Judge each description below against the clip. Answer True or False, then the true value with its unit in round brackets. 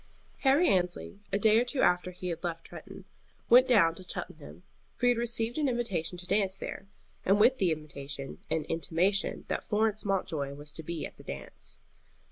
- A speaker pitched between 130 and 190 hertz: True (185 Hz)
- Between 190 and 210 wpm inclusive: True (195 wpm)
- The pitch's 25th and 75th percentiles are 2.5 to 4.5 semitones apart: False (5.4 semitones)